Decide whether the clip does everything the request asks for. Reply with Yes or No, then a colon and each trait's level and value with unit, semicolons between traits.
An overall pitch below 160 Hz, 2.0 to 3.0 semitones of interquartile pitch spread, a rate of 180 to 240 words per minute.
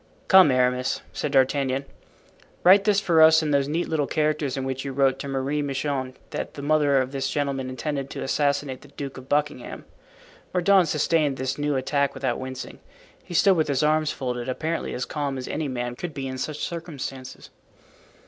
Yes: medium, 140 Hz; narrow, 2.6 semitones; average, 185 wpm